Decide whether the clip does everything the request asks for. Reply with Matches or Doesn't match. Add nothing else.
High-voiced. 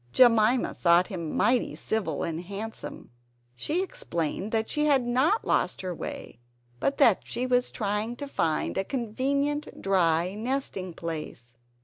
Matches